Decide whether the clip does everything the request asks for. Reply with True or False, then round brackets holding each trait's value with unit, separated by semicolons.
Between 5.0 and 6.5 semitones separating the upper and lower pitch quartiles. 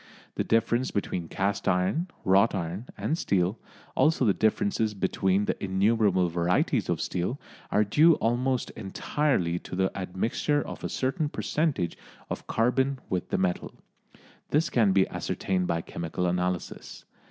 True (5.4 semitones)